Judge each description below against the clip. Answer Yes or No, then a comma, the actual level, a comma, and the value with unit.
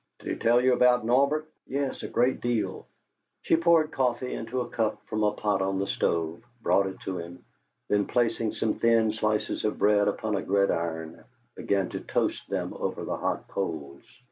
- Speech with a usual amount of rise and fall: Yes, average, 4.0 semitones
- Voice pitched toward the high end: No, low, 110 Hz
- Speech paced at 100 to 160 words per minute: No, average, 185 wpm